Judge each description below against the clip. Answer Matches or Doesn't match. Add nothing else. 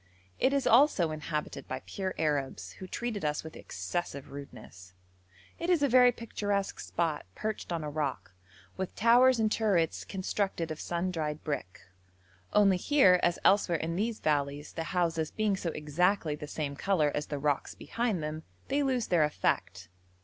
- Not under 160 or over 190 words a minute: Matches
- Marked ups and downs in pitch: Matches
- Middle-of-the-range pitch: Matches